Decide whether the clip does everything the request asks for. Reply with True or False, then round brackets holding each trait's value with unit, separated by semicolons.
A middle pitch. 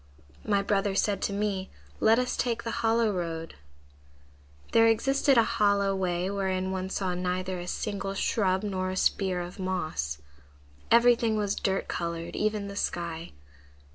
False (195 Hz)